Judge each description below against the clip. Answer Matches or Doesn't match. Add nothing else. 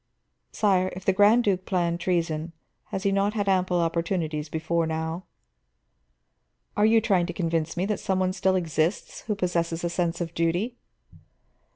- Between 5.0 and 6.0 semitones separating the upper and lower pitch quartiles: Doesn't match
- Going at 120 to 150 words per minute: Doesn't match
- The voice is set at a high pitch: Doesn't match